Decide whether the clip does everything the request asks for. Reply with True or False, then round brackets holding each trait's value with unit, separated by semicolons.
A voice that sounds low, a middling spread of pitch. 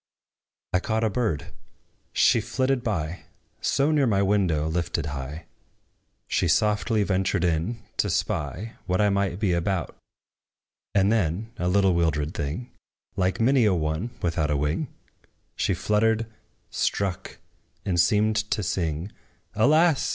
True (95 Hz; 4.6 semitones)